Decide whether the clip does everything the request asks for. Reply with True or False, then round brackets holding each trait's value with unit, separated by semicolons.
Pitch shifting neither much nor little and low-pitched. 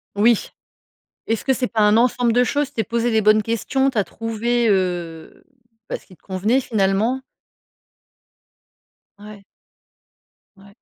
False (3.2 semitones; 225 Hz)